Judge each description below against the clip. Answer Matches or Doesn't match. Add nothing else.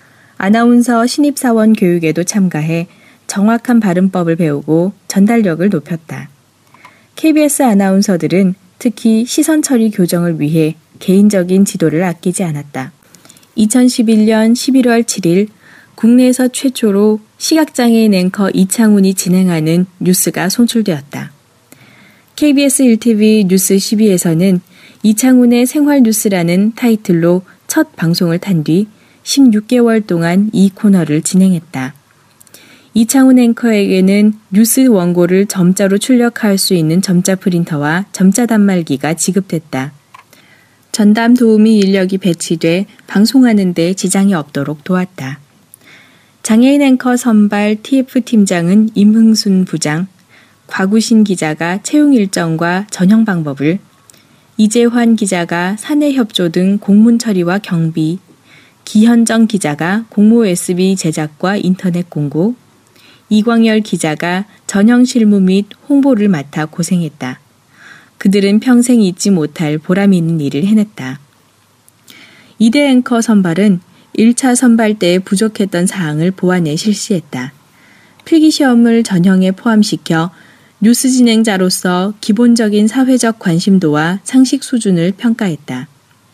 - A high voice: Matches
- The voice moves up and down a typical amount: Matches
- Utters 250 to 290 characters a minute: Matches